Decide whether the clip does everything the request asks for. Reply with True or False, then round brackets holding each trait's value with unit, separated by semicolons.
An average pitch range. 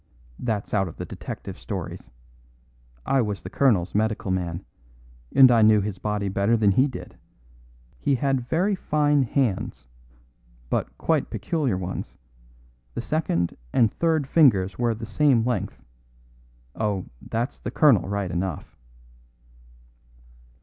False (5.7 semitones)